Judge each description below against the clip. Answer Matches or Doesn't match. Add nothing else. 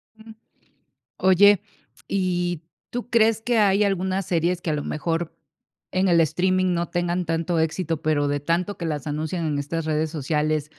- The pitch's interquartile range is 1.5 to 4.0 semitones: Matches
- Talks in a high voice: Doesn't match